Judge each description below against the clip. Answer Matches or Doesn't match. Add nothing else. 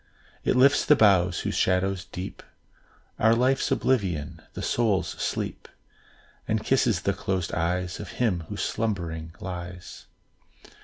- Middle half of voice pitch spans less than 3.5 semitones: Doesn't match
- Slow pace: Matches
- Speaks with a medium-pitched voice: Doesn't match